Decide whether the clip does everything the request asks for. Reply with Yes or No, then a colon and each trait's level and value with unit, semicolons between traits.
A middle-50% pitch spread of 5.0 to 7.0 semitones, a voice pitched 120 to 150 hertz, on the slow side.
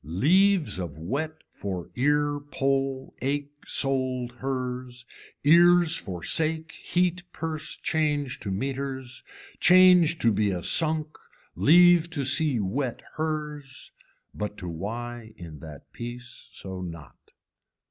Yes: wide, 5.5 semitones; low, 135 Hz; slow, 115 wpm